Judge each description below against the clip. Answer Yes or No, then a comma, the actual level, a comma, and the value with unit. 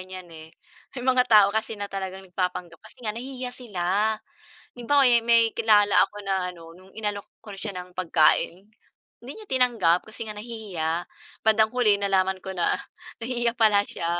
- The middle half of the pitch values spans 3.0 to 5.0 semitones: Yes, average, 3.8 semitones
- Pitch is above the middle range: Yes, high, 205 Hz